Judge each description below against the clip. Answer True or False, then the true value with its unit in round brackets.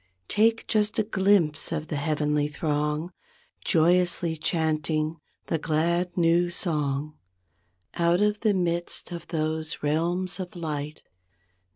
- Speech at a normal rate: False (115 wpm)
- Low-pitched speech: False (165 Hz)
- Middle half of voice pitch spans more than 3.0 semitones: False (2.6 semitones)